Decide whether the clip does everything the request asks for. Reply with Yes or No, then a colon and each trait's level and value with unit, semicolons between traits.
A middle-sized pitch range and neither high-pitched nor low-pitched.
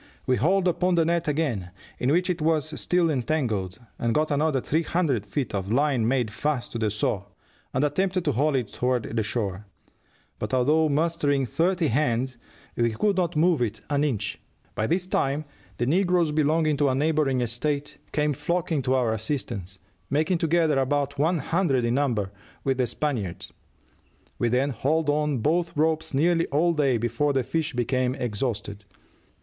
Yes: average, 4.8 semitones; medium, 145 Hz